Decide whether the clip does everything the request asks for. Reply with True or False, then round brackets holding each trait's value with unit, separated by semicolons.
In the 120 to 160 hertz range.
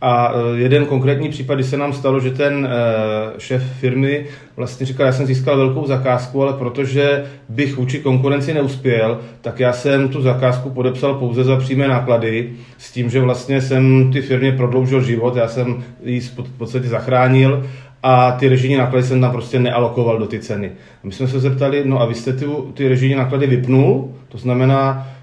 True (130 Hz)